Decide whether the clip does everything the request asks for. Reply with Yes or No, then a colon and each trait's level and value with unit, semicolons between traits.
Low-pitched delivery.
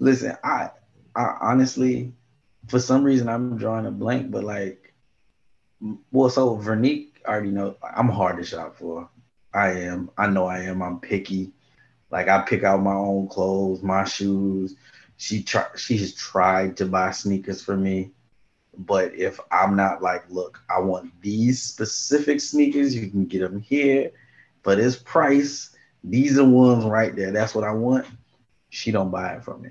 Yes: low, 100 Hz